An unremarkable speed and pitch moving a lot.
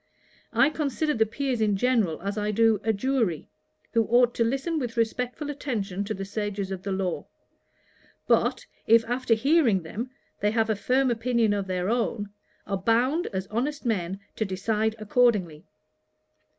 No: average, 165 wpm; average, 3.8 semitones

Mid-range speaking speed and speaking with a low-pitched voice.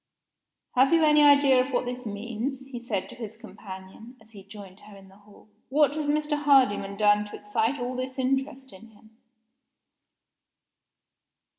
No: average, 165 wpm; high, 240 Hz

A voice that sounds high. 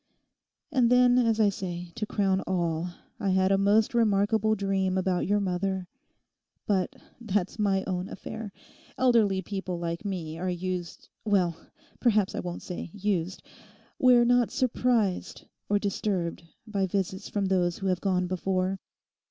Yes: high, 195 Hz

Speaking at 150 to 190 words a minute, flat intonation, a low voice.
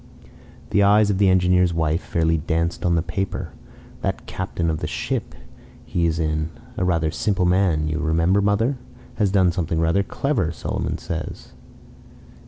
No: average, 160 wpm; average, 3.0 semitones; very low, 85 Hz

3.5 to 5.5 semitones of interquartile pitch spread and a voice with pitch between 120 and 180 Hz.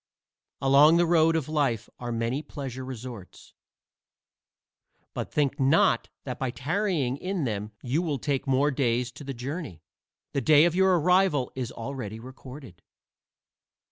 Yes: average, 4.0 semitones; low, 135 Hz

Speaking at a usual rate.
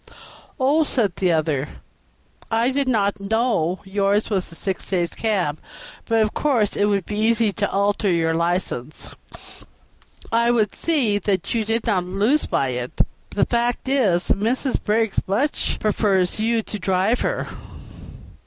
Yes: average, 155 wpm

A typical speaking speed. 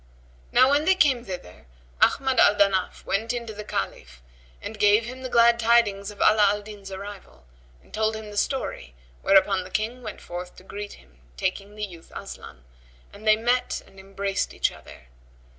Yes: average, 180 wpm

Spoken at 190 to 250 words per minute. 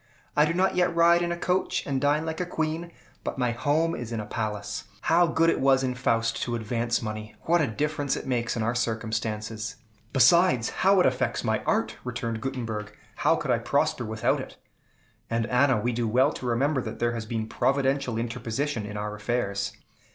Yes: average, 200 wpm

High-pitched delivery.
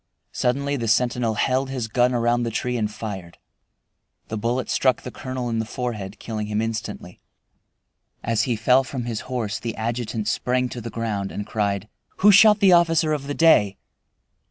No: low, 120 Hz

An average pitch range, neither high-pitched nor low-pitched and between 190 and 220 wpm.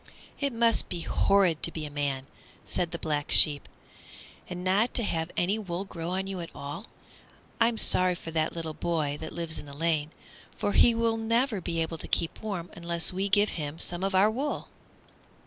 Yes: average, 4.0 semitones; medium, 175 Hz; average, 200 wpm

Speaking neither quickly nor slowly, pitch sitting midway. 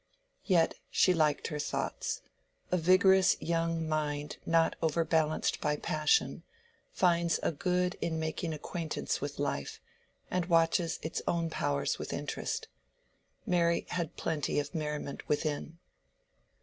No: slow, 125 wpm; medium, 165 Hz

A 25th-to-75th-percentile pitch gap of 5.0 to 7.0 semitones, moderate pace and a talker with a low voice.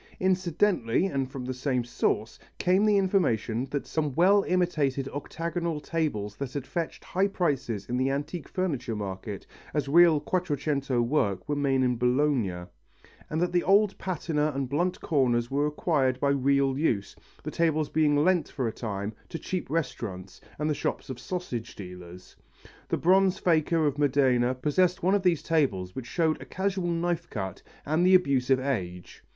No: wide, 5.6 semitones; average, 170 wpm; medium, 145 Hz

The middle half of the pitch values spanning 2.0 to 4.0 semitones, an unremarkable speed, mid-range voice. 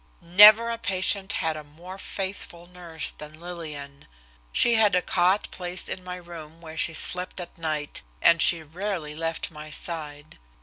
Yes: average, 2.9 semitones; average, 160 wpm; medium, 170 Hz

